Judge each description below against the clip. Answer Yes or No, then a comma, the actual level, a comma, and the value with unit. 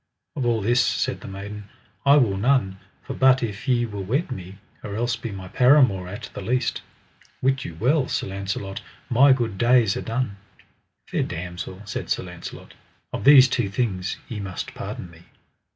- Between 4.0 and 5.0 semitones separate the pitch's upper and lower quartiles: Yes, average, 4.7 semitones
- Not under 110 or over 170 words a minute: No, average, 180 wpm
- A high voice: No, low, 110 Hz